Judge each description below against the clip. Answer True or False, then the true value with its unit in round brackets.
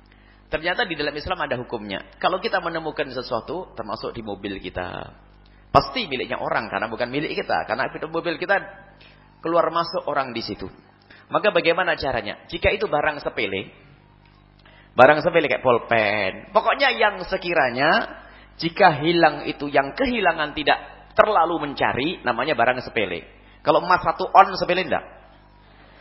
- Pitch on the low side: False (155 Hz)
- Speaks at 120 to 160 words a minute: True (140 wpm)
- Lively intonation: True (7.8 semitones)